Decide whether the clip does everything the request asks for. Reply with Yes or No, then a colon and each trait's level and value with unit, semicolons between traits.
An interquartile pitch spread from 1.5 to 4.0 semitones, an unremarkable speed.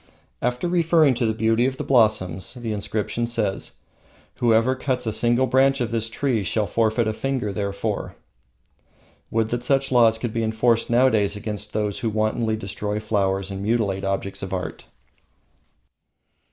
Yes: average, 2.8 semitones; average, 155 wpm